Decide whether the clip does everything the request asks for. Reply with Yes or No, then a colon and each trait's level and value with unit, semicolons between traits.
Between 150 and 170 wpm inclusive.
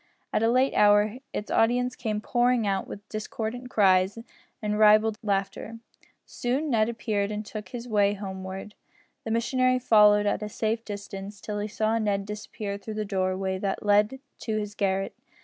Yes: average, 165 wpm